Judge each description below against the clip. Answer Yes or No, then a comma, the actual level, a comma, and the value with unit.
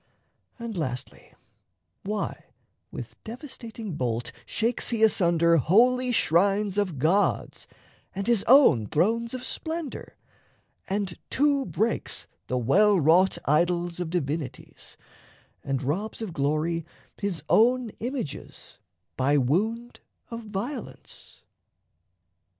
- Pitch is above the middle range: Yes, high, 195 Hz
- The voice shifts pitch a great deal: Yes, wide, 6.5 semitones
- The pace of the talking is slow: Yes, slow, 105 wpm